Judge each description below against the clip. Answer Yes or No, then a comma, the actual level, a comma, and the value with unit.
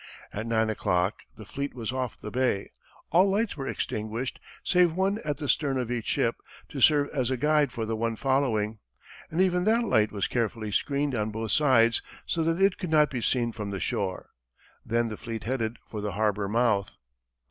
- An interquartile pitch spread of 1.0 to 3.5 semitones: No, average, 5.3 semitones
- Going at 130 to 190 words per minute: No, average, 200 wpm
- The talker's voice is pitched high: No, low, 120 Hz